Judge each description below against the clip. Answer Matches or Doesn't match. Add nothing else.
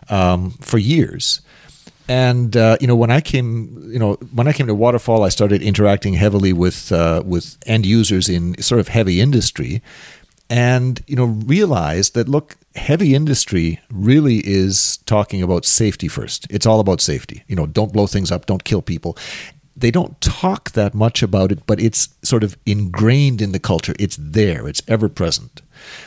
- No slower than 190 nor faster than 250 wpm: Doesn't match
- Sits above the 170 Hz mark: Doesn't match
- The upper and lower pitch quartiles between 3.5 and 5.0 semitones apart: Matches